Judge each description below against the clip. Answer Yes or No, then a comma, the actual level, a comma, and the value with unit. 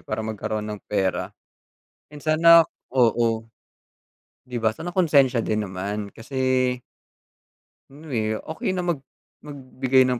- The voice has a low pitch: Yes, low, 130 Hz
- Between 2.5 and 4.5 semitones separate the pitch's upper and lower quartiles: No, average, 5.0 semitones